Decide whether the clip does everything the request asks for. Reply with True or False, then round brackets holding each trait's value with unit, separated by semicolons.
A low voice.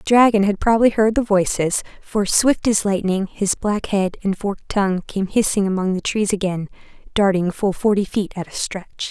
False (200 Hz)